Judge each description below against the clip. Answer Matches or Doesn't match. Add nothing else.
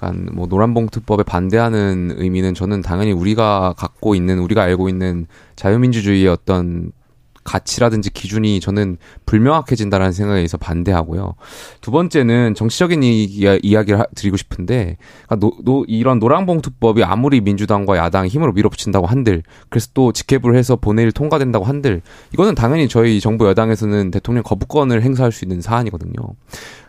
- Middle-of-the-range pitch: Doesn't match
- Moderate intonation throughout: Matches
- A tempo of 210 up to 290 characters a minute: Doesn't match